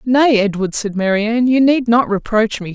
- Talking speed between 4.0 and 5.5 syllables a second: Yes, 4.8 syllables/s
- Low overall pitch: No, high, 225 Hz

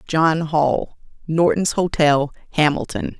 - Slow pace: Yes, slow, 95 wpm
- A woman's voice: Yes, female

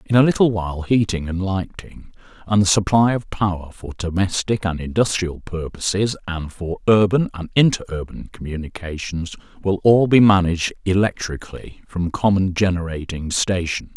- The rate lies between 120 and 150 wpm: Yes, average, 140 wpm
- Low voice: Yes, very low, 95 Hz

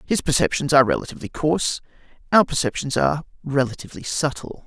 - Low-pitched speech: No, medium, 145 Hz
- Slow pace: Yes, slow, 130 wpm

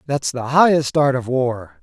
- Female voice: No, male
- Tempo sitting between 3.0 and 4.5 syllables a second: Yes, 4.2 syllables/s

